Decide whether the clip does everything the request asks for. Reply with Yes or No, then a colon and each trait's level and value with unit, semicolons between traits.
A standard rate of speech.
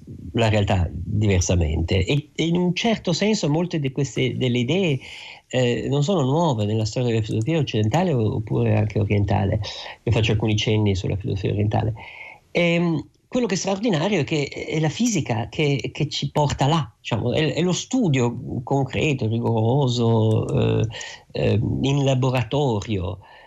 Yes: average, 150 wpm